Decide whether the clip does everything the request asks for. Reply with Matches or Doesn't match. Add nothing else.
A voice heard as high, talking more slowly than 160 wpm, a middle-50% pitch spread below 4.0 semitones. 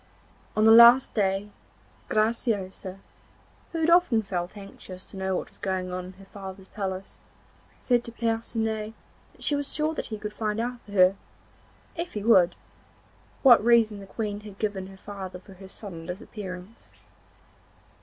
Doesn't match